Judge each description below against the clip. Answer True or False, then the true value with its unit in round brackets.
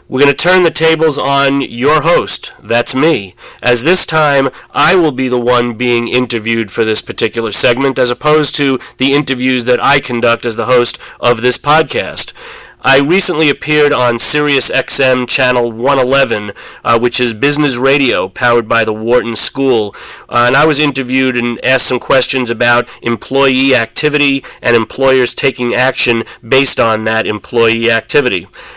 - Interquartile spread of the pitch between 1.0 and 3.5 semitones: True (2.6 semitones)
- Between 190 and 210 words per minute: False (165 wpm)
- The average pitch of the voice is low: True (125 Hz)